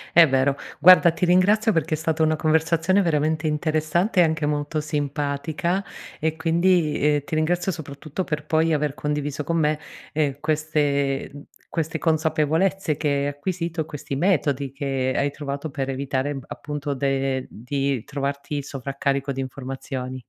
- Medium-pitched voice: Yes, medium, 150 Hz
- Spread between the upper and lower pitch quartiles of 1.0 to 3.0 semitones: Yes, narrow, 2.5 semitones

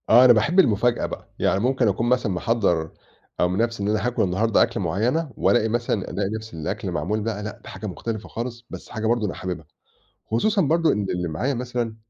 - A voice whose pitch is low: Yes, low, 110 Hz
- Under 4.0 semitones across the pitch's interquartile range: Yes, average, 3.4 semitones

